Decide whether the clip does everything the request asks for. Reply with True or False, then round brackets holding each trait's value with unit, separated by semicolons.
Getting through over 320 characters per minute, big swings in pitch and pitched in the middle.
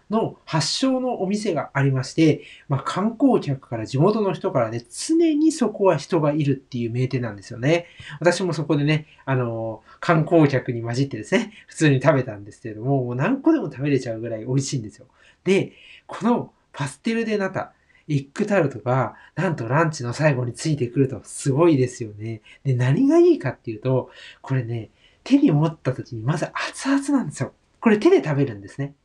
True (380 characters per minute; 7.1 semitones; 145 Hz)